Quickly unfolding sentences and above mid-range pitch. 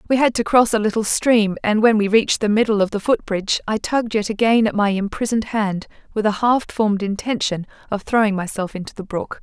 Yes: fast, 230 wpm; high, 215 Hz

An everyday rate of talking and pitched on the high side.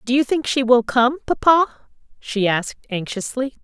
Yes: average, 165 wpm; very high, 250 Hz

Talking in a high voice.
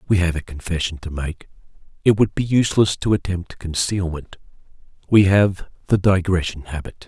No: very low, 90 Hz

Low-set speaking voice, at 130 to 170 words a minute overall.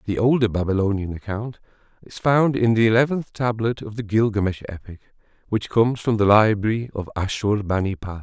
Yes: low, 110 Hz; average, 155 wpm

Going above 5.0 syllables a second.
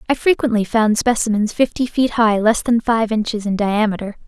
Yes: 5.2 syllables/s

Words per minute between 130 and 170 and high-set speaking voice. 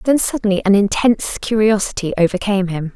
Yes: average, 140 wpm; high, 205 Hz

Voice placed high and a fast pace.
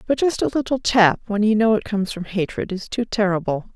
Yes: high, 210 Hz; fast, 240 wpm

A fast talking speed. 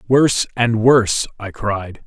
No: average, 145 wpm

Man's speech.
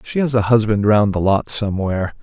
Yes: male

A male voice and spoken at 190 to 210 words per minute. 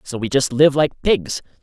No: male; fast, 220 wpm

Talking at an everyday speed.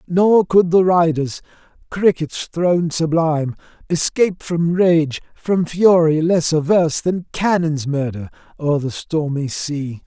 No: slow, 125 wpm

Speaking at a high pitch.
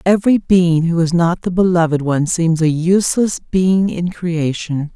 No: medium, 175 Hz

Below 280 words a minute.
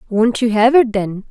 Yes: fast, 230 wpm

